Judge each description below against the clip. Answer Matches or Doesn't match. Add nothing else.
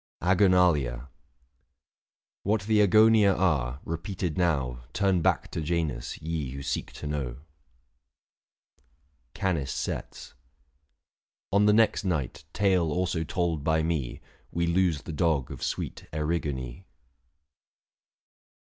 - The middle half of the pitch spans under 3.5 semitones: Doesn't match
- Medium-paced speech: Doesn't match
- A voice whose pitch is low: Matches